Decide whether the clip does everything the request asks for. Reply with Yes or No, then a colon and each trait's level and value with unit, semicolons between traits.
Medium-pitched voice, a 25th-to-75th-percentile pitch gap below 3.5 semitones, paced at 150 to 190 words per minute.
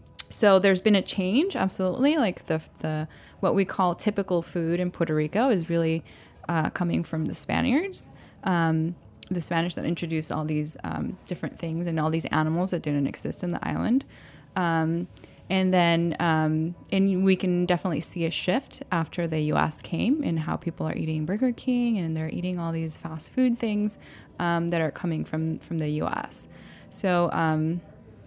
Yes: medium, 170 Hz; average, 3.1 semitones; average, 180 wpm